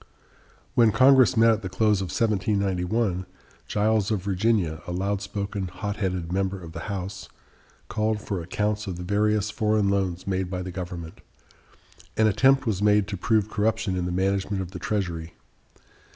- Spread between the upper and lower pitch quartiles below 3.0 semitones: Yes, narrow, 2.6 semitones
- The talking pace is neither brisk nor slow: Yes, average, 165 wpm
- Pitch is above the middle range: No, low, 100 Hz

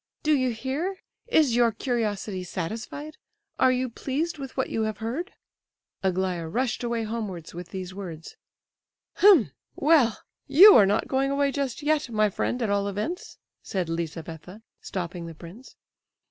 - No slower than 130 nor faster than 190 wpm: Yes, average, 150 wpm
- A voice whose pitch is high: Yes, high, 225 Hz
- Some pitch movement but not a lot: No, wide, 6.5 semitones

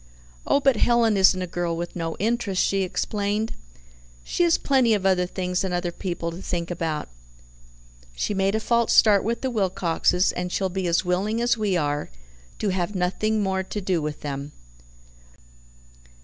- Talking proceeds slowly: No, average, 175 wpm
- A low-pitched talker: No, high, 190 Hz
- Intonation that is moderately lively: Yes, average, 3.5 semitones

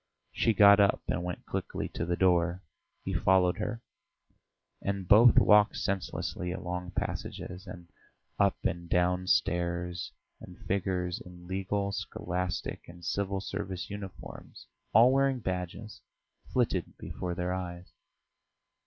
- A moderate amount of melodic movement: No, narrow, 2.1 semitones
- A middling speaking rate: No, slow, 125 wpm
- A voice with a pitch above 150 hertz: No, very low, 90 Hz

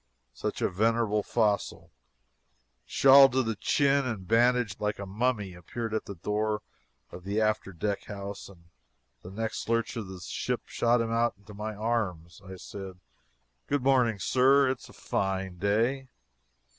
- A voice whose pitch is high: No, low, 105 Hz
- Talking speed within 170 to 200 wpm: No, average, 155 wpm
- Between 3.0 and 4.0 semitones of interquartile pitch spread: Yes, average, 3.4 semitones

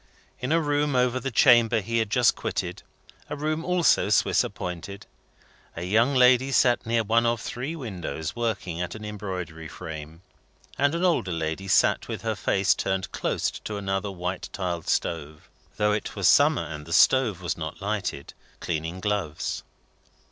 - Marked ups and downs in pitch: Yes, wide, 5.9 semitones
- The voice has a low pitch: Yes, low, 105 Hz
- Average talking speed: Yes, average, 165 wpm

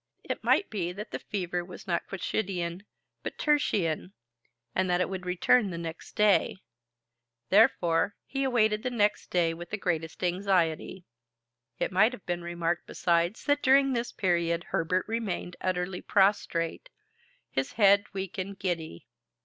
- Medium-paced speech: Yes, average, 145 wpm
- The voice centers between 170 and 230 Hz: Yes, medium, 185 Hz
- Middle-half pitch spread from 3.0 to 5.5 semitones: Yes, average, 3.3 semitones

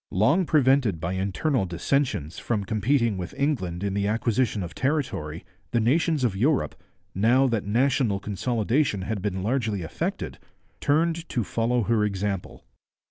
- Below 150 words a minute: Yes, average, 140 wpm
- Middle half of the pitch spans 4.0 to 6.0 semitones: Yes, wide, 5.4 semitones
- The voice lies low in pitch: Yes, low, 110 Hz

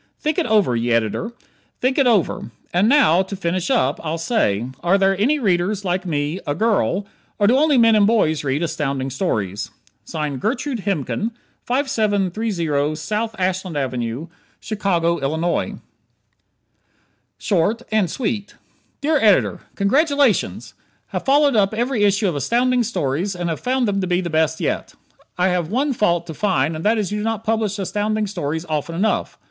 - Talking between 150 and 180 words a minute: Yes, average, 160 wpm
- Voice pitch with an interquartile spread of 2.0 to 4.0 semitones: No, wide, 5.6 semitones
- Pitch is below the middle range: No, high, 195 Hz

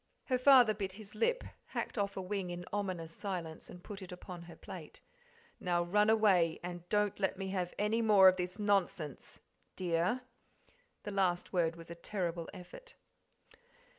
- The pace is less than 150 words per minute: No, average, 165 wpm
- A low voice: No, high, 190 Hz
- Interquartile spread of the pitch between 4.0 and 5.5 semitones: No, average, 3.0 semitones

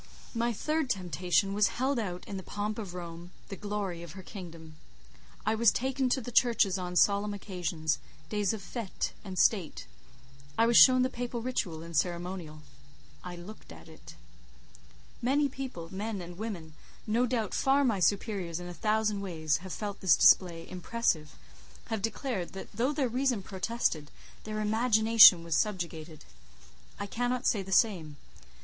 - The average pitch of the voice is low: No, high, 200 Hz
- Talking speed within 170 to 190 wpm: No, average, 155 wpm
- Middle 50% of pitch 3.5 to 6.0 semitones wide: Yes, average, 4.6 semitones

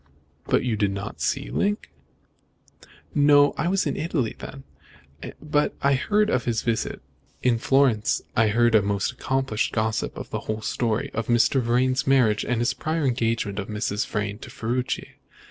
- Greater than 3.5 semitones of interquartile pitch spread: Yes, average, 3.9 semitones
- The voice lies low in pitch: Yes, low, 120 Hz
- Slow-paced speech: No, average, 165 wpm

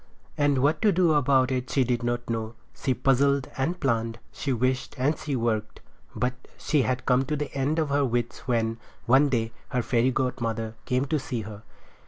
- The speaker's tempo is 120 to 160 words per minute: No, average, 195 wpm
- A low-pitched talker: Yes, low, 130 Hz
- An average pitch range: Yes, average, 3.0 semitones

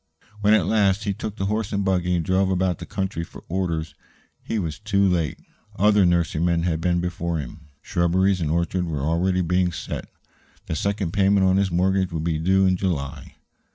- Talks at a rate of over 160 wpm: Yes, average, 195 wpm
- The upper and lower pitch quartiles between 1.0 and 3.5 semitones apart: Yes, narrow, 2.5 semitones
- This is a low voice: Yes, very low, 90 Hz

